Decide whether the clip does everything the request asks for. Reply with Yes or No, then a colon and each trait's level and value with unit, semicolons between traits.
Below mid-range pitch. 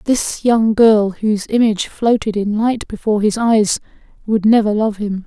No: high, 215 Hz